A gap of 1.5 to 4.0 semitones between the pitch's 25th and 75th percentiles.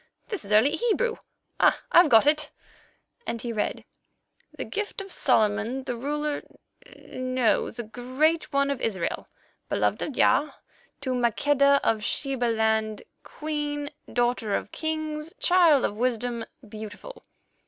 No: average, 4.9 semitones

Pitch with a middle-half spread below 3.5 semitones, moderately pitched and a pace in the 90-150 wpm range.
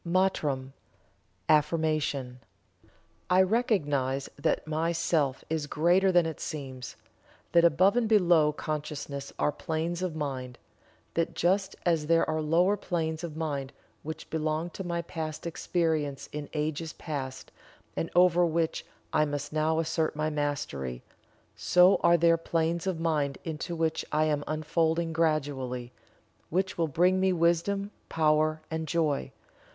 Yes: narrow, 2.4 semitones; medium, 160 Hz; slow, 135 wpm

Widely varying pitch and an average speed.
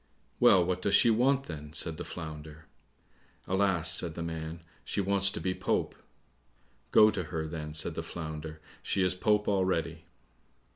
No: average, 3.7 semitones; average, 160 wpm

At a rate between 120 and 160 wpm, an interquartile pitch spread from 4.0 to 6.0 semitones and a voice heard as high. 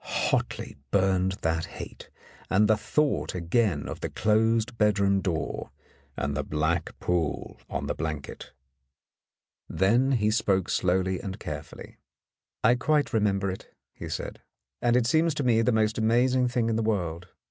No: average, 150 wpm; average, 4.3 semitones; low, 105 Hz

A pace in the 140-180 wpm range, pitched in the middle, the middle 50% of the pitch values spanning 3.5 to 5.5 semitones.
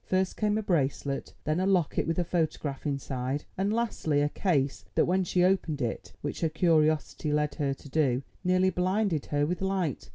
No: average, 190 wpm; medium, 160 Hz; average, 4.4 semitones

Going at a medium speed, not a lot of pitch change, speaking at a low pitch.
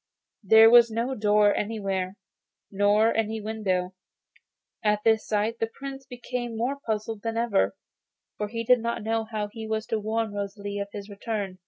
No: average, 165 wpm; narrow, 1.9 semitones; high, 220 Hz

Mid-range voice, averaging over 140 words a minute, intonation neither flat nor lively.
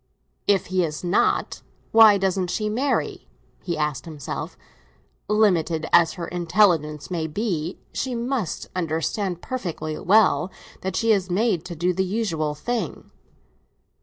No: medium, 180 Hz; slow, 135 wpm; average, 4.6 semitones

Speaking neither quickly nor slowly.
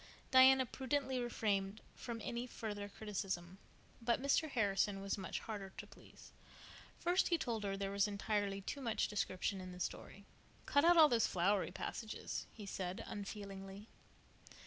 Yes: average, 150 wpm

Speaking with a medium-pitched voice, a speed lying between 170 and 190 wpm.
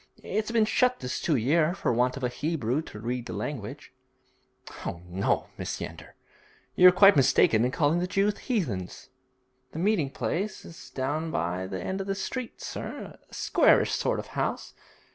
Yes: medium, 155 Hz; average, 175 wpm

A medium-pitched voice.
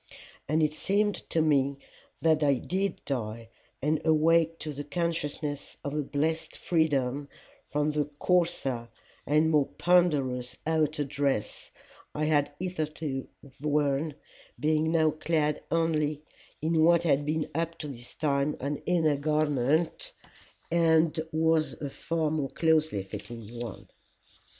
Yes: medium, 155 Hz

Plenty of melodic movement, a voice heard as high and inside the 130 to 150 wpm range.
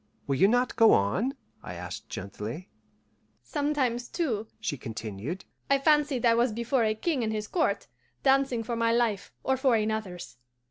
No: wide, 6.1 semitones; high, 230 Hz; average, 160 wpm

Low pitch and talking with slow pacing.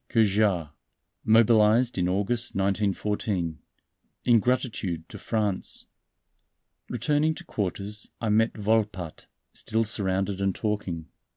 Yes: low, 105 Hz; slow, 100 wpm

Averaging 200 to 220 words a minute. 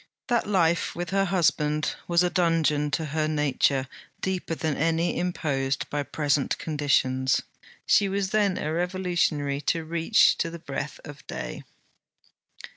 No: average, 140 wpm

